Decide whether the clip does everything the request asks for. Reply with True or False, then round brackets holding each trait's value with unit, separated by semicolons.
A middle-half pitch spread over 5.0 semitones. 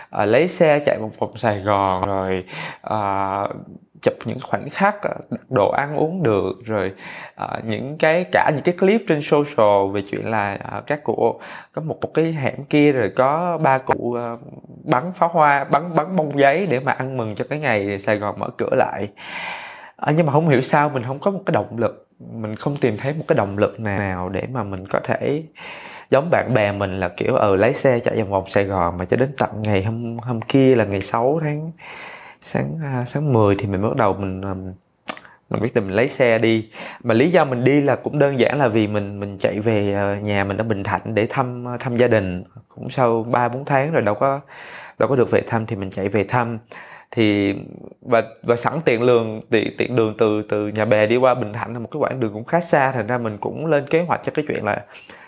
True (5.5 semitones)